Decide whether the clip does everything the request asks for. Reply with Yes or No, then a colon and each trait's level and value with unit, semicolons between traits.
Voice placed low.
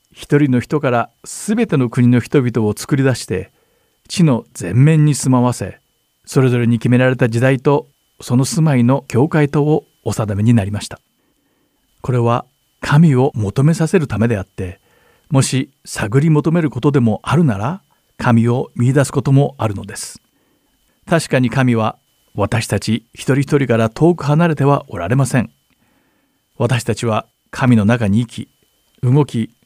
Yes: low, 125 Hz